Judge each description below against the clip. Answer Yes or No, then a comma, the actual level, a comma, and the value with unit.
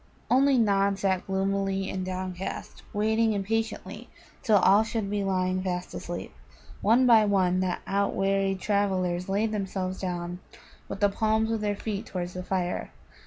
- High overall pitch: Yes, high, 195 Hz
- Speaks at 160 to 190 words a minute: No, average, 150 wpm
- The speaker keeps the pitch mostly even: Yes, narrow, 2.3 semitones